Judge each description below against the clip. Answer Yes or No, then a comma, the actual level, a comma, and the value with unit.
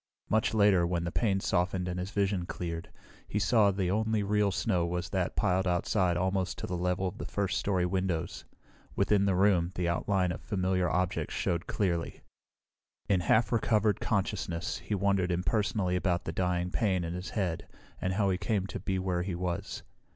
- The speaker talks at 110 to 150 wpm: No, average, 185 wpm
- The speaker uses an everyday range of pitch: No, narrow, 2.2 semitones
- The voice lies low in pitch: Yes, very low, 95 Hz